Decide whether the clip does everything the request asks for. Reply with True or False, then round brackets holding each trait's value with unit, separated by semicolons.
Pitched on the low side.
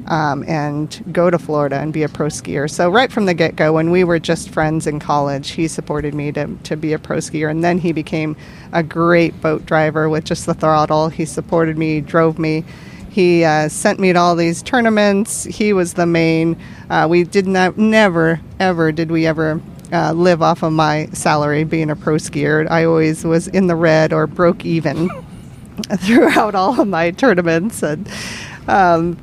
False (165 Hz)